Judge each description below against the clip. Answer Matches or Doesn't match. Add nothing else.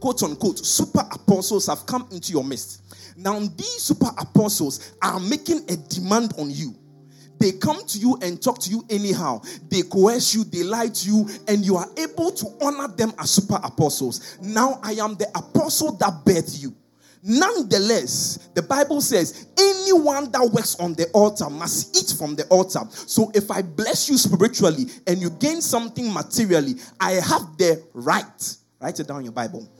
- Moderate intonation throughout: Doesn't match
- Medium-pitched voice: Doesn't match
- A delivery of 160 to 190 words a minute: Matches